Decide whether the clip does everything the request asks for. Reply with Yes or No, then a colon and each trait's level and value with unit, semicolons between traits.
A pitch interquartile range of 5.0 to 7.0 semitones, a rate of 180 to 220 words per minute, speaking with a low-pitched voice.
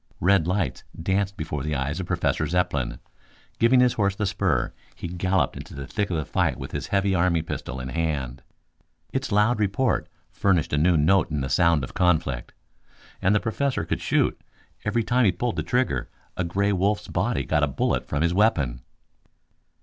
Yes: average, 5.3 semitones; average, 190 wpm; very low, 90 Hz